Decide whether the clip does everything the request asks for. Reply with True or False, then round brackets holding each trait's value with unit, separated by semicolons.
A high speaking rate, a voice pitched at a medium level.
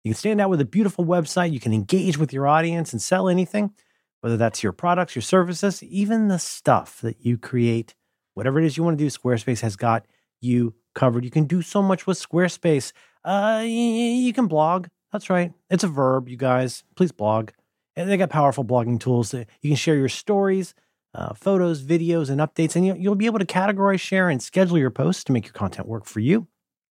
True (210 wpm; 165 Hz)